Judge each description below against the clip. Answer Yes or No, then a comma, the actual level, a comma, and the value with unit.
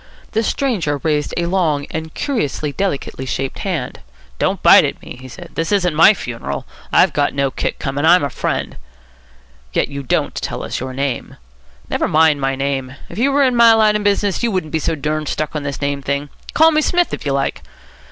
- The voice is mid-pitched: Yes, medium, 155 Hz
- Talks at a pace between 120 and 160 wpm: No, fast, 205 wpm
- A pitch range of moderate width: No, wide, 6.2 semitones